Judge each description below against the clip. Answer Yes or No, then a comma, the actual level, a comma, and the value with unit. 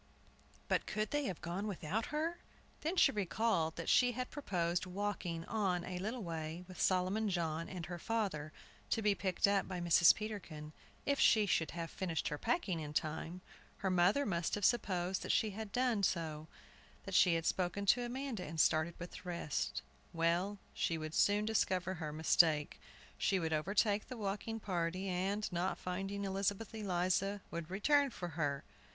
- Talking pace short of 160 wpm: No, average, 175 wpm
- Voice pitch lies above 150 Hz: Yes, medium, 185 Hz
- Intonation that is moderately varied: Yes, average, 3.9 semitones